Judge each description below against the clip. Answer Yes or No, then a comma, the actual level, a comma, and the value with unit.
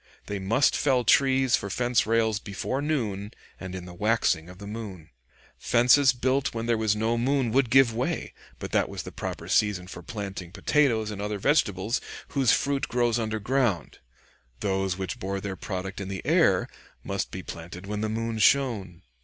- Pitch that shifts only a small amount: No, average, 4.2 semitones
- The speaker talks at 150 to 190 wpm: Yes, average, 180 wpm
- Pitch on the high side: No, low, 110 Hz